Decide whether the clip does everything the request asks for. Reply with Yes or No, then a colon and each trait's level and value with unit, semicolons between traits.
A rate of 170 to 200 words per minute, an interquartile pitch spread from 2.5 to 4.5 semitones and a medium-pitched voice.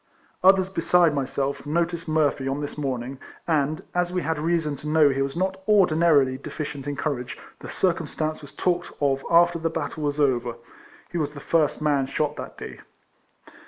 Yes: average, 175 wpm; average, 3.3 semitones; medium, 150 Hz